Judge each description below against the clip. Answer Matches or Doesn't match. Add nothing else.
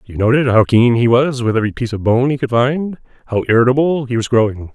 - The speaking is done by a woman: Doesn't match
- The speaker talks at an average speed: Doesn't match